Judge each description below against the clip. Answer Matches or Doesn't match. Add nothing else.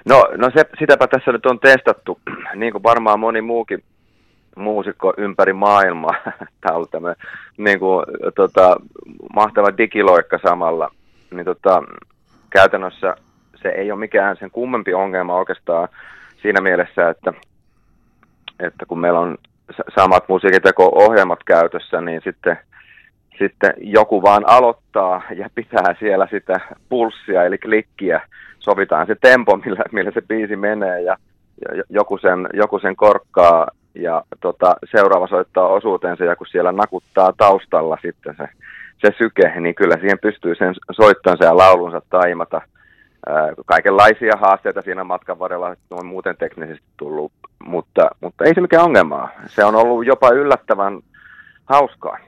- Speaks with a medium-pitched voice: Doesn't match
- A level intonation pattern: Doesn't match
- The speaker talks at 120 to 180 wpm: Matches